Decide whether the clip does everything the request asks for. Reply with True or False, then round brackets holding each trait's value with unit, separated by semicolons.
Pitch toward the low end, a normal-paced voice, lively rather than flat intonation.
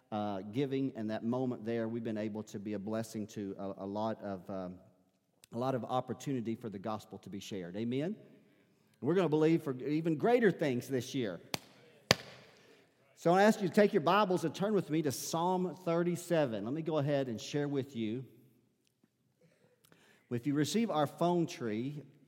True (130 Hz; 190 wpm; 6.5 semitones)